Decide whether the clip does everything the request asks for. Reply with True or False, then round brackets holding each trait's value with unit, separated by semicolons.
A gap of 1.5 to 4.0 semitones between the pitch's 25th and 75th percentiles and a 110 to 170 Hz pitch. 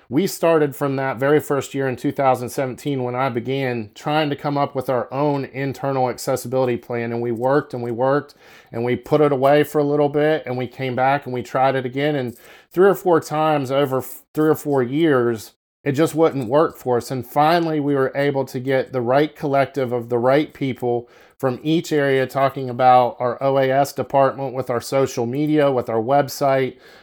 True (2.4 semitones; 135 Hz)